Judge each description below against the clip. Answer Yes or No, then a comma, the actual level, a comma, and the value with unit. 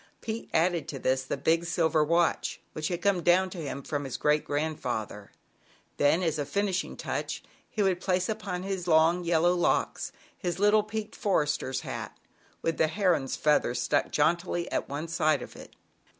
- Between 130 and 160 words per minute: No, average, 175 wpm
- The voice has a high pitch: No, medium, 170 Hz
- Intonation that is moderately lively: Yes, average, 3.7 semitones